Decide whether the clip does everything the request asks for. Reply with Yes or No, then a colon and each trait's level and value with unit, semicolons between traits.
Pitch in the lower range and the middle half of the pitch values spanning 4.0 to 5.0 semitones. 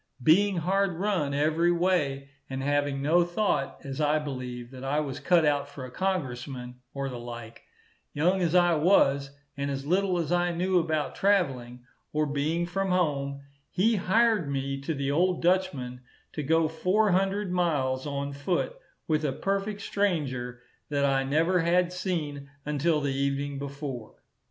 No: medium, 150 Hz; average, 4.6 semitones